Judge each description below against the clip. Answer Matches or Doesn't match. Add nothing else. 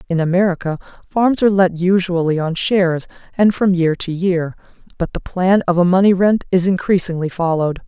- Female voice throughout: Matches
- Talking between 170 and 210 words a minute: Matches